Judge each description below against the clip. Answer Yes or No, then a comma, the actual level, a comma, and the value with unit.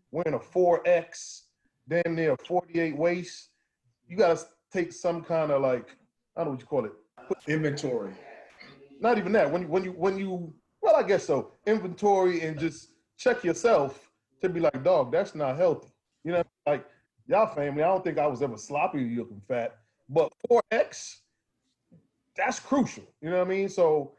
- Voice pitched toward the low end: No, medium, 170 Hz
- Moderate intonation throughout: Yes, average, 3.9 semitones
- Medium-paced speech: Yes, average, 180 wpm